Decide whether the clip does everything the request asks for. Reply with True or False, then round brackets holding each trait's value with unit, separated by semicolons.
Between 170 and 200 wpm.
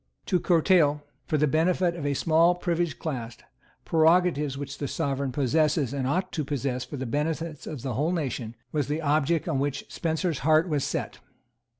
True (180 wpm)